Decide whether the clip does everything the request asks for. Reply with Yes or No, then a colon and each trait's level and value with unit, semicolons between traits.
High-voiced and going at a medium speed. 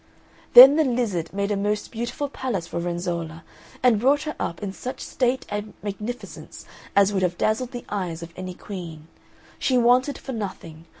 Yes: high, 205 Hz; average, 175 wpm